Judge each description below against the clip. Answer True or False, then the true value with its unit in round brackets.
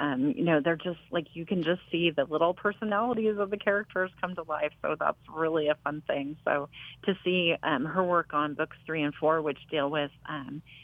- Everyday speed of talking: False (220 wpm)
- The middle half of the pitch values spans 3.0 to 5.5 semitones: True (3.6 semitones)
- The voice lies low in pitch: False (160 Hz)